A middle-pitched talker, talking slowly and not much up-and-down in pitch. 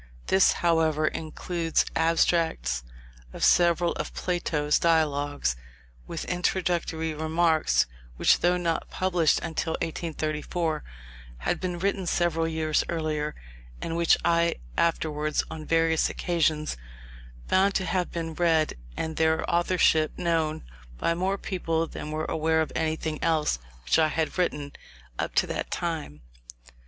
Yes: medium, 165 Hz; slow, 125 wpm; narrow, 1.7 semitones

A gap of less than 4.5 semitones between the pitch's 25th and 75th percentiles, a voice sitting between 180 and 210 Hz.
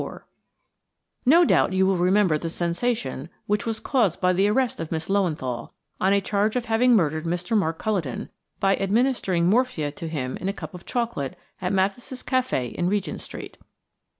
No: average, 5.0 semitones; high, 190 Hz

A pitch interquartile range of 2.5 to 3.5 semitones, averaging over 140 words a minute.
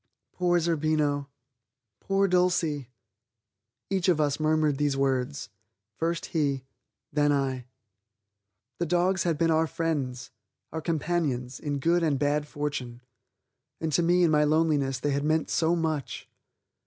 No: average, 2.9 semitones; slow, 135 wpm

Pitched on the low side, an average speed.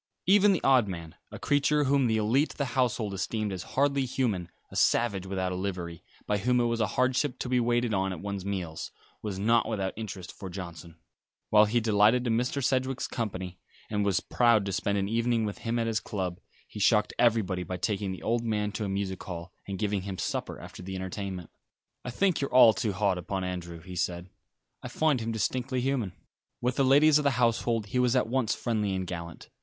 No: low, 105 Hz; fast, 215 wpm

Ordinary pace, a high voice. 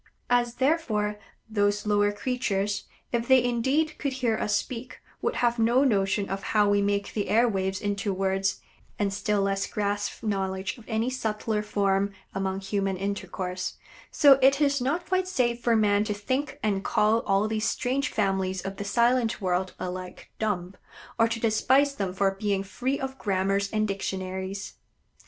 Yes: average, 165 wpm; high, 210 Hz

